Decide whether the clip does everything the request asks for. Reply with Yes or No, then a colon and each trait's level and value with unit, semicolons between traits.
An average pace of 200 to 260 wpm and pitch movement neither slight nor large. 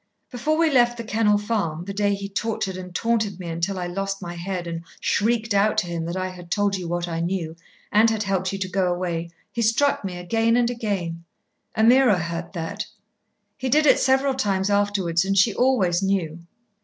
Yes: fast, 205 wpm; average, 4.2 semitones